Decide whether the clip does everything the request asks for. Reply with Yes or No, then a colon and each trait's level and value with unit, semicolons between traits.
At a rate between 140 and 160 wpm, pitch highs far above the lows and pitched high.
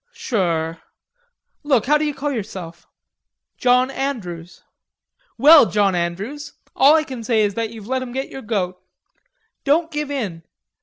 Yes: average, 150 wpm; wide, 6.8 semitones; high, 235 Hz